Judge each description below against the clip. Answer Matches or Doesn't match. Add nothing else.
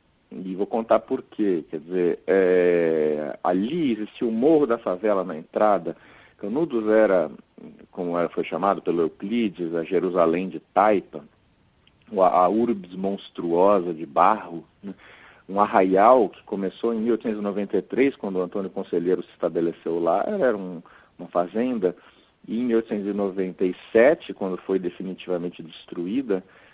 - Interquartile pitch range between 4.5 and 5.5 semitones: Doesn't match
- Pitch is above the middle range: Doesn't match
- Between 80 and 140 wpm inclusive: Matches